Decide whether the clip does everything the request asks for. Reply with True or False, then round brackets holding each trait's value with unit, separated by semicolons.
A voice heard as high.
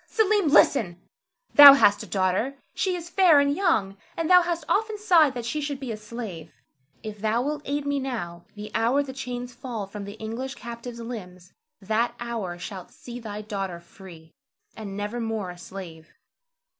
True (230 Hz)